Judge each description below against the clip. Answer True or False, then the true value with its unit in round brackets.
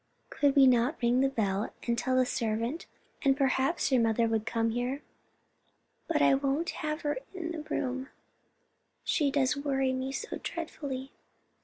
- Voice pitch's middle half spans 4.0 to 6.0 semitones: False (3.1 semitones)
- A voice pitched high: True (265 Hz)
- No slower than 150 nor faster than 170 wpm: True (160 wpm)